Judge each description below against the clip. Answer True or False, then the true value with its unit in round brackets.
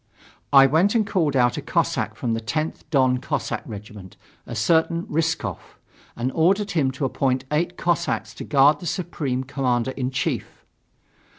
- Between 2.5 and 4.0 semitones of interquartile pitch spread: False (4.6 semitones)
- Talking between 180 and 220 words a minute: False (160 wpm)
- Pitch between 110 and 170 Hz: True (140 Hz)